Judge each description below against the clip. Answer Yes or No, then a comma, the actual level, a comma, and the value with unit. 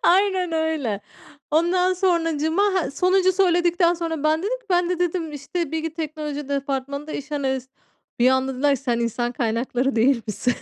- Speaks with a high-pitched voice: Yes, very high, 310 Hz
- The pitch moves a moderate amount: Yes, average, 4.8 semitones